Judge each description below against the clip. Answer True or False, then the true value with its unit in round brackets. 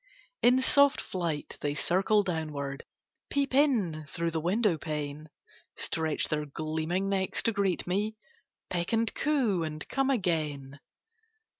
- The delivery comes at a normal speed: False (130 wpm)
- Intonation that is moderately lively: False (5.9 semitones)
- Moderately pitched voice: True (175 Hz)